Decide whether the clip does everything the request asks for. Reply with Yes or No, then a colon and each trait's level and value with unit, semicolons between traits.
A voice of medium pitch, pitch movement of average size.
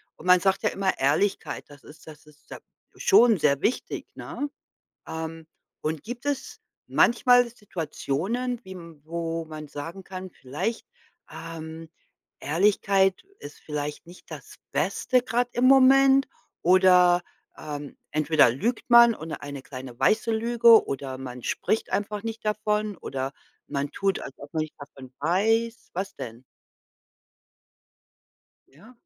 No: medium, 180 Hz; wide, 7.0 semitones